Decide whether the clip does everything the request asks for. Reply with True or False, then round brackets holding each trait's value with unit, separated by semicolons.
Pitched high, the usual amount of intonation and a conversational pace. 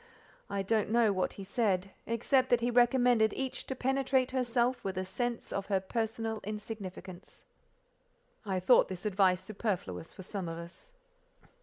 True (215 Hz; 4.3 semitones; 165 wpm)